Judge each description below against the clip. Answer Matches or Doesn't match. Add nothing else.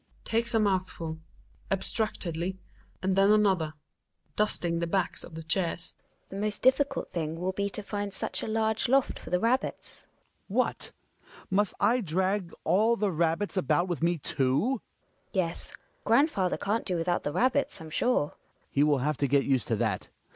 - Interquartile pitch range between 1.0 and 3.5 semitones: Doesn't match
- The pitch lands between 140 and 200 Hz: Matches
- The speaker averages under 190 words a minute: Doesn't match